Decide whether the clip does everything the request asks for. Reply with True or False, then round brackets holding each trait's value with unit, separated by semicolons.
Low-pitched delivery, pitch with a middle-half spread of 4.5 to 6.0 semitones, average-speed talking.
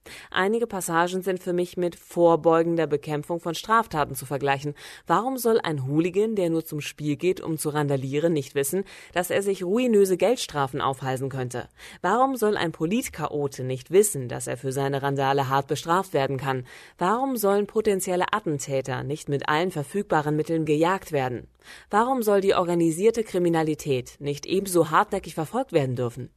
False (165 Hz; 5.2 semitones; 160 wpm)